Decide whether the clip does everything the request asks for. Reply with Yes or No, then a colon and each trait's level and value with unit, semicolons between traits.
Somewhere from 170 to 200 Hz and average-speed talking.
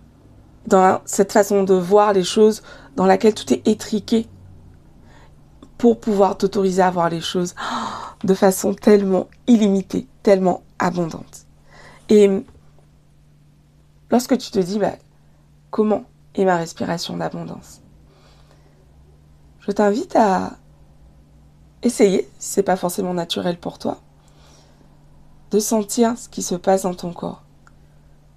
No: medium, 185 Hz; slow, 125 wpm